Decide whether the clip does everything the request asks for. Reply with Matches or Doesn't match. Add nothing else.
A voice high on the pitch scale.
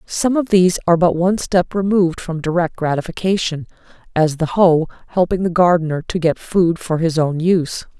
Doesn't match